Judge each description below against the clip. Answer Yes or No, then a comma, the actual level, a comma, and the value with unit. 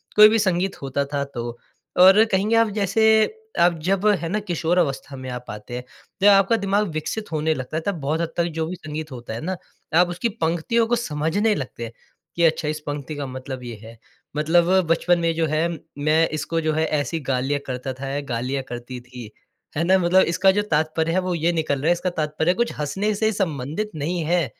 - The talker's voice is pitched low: No, medium, 160 Hz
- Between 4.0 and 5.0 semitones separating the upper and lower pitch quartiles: Yes, average, 4.7 semitones